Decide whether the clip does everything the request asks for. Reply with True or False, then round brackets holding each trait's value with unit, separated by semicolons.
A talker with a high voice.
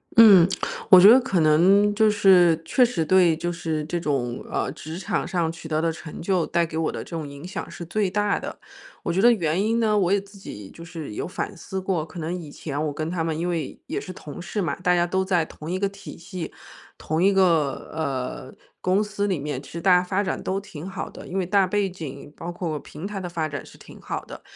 False (175 Hz)